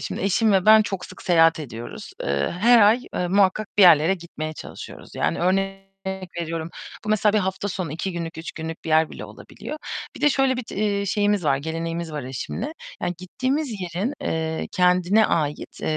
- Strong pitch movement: No, average, 4.2 semitones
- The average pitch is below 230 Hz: Yes, medium, 185 Hz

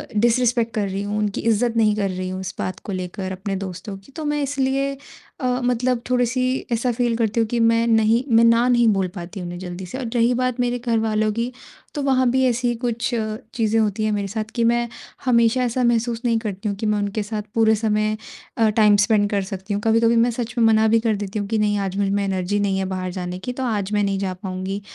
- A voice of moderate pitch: No, high, 220 Hz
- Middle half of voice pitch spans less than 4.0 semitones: Yes, average, 3.1 semitones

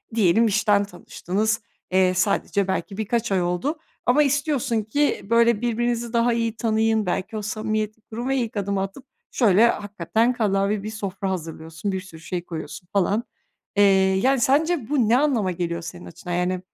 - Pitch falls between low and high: No, high, 215 Hz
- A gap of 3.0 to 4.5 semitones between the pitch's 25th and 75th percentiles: Yes, average, 3.9 semitones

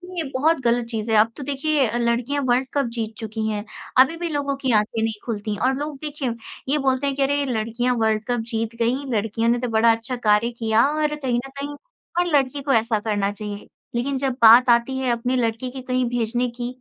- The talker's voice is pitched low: No, high, 245 Hz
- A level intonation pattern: No, average, 3.2 semitones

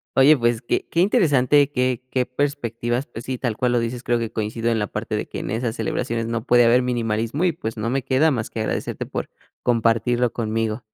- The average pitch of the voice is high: No, low, 120 Hz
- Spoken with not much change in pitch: Yes, narrow, 2.2 semitones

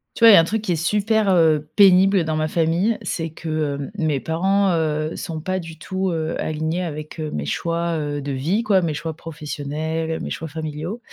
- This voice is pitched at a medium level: Yes, medium, 160 Hz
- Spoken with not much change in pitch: No, average, 3.2 semitones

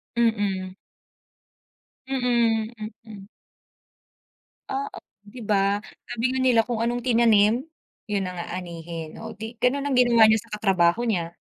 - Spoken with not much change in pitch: No, average, 3.7 semitones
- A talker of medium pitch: No, high, 220 Hz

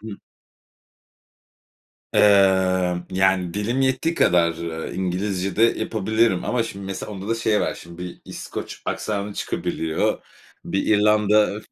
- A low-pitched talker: Yes, low, 100 Hz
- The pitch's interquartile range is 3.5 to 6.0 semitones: No, average, 2.8 semitones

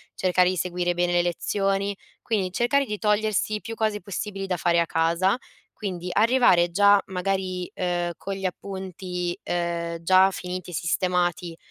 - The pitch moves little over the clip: Yes, narrow, 2.3 semitones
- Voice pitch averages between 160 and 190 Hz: Yes, medium, 185 Hz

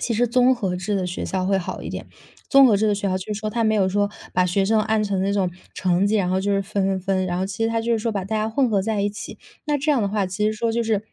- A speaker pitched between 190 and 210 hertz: Yes, high, 205 Hz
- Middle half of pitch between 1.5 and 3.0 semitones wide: Yes, narrow, 2.6 semitones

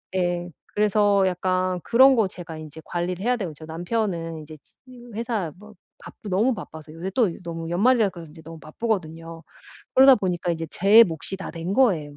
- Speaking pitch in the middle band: Yes, medium, 180 Hz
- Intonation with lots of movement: No, average, 4.5 semitones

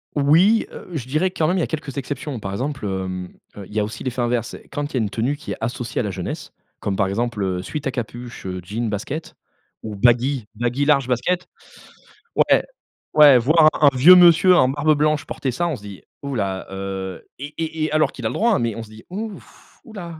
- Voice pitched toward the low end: Yes, low, 130 Hz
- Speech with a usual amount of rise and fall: No, wide, 6.2 semitones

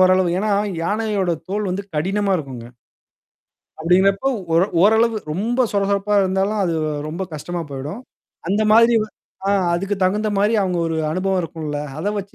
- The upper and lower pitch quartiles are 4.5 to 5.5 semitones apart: No, average, 3.2 semitones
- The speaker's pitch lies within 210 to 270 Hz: No, high, 195 Hz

